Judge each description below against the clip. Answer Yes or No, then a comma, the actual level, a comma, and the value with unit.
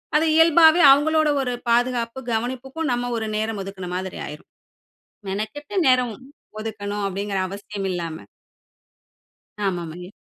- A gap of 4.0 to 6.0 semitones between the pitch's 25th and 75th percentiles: Yes, average, 5.2 semitones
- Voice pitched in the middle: No, high, 220 Hz